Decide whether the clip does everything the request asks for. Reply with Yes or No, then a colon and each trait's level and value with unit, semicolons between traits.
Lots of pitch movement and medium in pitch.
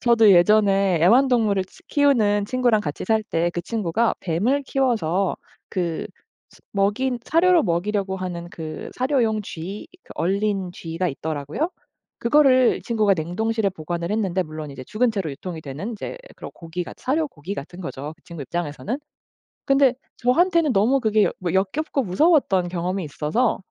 No: wide, 5.9 semitones; high, 200 Hz